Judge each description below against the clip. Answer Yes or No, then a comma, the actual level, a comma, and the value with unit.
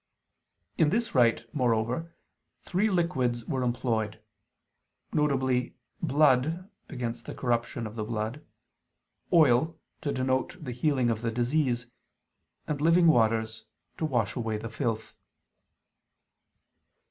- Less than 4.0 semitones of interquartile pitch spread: No, average, 4.7 semitones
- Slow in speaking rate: Yes, slow, 110 wpm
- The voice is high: No, low, 125 Hz